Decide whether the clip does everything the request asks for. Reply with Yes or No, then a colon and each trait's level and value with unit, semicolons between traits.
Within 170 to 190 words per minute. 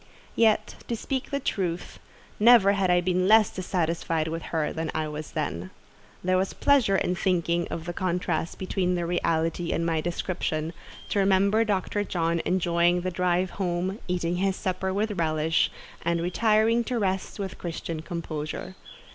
No: average, 155 wpm